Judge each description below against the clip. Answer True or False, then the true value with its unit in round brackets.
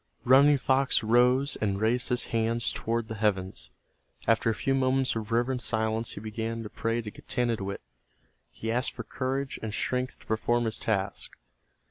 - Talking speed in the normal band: True (165 wpm)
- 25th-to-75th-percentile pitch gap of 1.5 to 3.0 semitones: True (2.4 semitones)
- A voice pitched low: True (115 Hz)